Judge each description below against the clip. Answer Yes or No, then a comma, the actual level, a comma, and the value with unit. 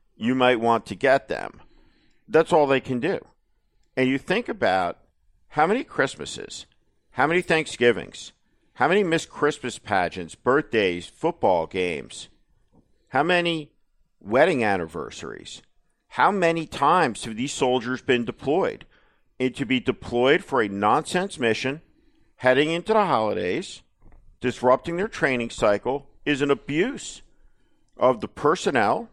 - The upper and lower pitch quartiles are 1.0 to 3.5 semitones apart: No, average, 5.3 semitones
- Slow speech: Yes, slow, 130 wpm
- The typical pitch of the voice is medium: No, low, 130 Hz